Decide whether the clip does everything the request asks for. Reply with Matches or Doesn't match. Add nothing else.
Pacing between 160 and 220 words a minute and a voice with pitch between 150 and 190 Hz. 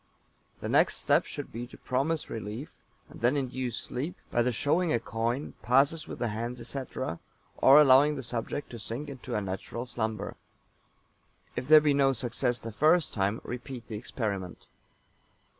Doesn't match